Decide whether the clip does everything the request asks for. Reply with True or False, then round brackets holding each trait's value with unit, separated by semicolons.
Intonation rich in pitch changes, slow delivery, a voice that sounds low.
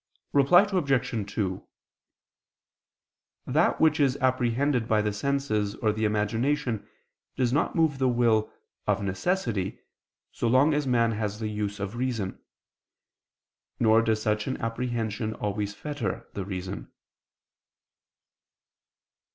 False (4.1 semitones; 120 wpm; 115 Hz)